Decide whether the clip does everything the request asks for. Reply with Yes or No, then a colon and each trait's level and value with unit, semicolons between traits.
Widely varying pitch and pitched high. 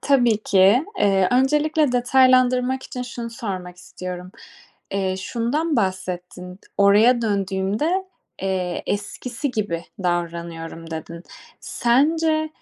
Yes: wide, 5.7 semitones; high, 210 Hz